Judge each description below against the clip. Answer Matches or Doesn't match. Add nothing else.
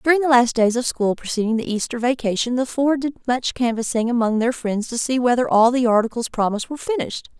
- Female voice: Matches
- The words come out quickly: Matches